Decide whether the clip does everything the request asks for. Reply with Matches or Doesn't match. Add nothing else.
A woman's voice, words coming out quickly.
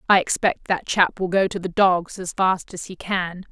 Matches